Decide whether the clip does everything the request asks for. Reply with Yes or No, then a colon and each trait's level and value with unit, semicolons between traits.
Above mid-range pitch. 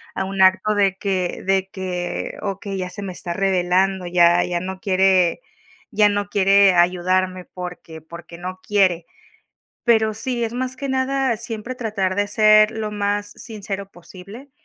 Yes: high, 195 Hz